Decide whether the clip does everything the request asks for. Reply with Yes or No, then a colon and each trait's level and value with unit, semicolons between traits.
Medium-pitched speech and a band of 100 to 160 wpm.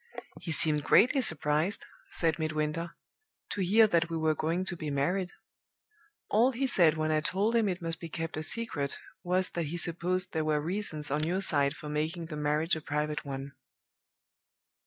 No: medium, 165 Hz; average, 180 wpm